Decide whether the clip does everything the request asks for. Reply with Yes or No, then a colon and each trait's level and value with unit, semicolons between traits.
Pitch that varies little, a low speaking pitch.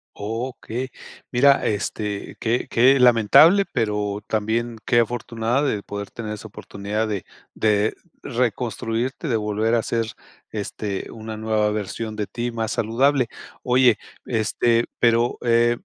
Yes: narrow, 2.3 semitones; low, 115 Hz